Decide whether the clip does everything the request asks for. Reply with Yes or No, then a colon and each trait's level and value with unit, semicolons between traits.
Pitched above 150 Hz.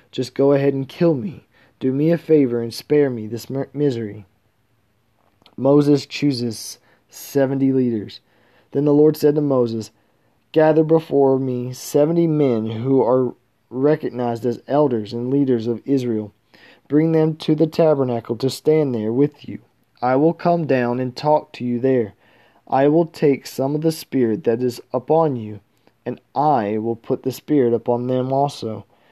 No: low, 130 Hz